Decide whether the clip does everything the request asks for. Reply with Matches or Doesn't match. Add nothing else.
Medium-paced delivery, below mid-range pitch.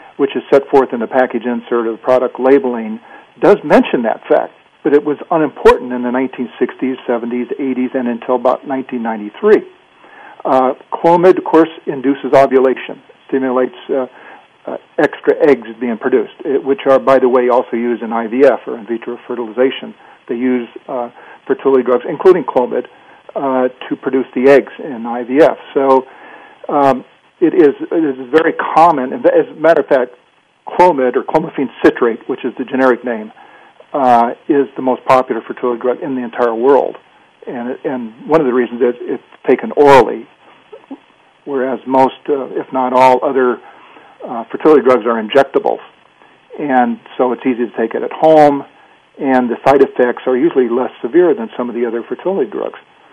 Matches